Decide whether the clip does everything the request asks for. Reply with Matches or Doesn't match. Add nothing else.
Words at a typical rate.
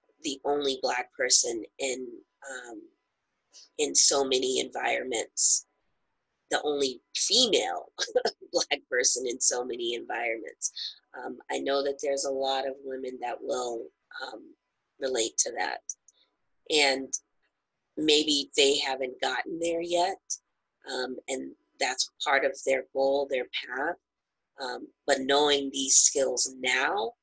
Doesn't match